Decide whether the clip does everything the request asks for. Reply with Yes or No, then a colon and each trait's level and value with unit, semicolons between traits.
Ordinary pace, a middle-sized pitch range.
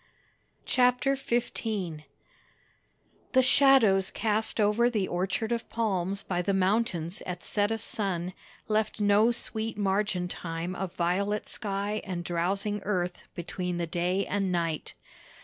No: slow, 130 wpm; average, 3.5 semitones